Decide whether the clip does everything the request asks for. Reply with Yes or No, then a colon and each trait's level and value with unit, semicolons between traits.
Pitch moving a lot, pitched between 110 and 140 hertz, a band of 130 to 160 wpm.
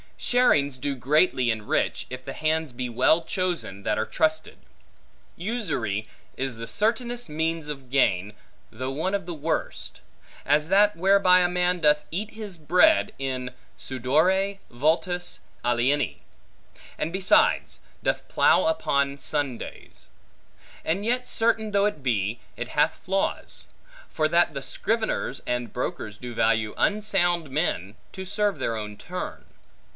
No: wide, 7.1 semitones; medium, 155 Hz; slow, 135 wpm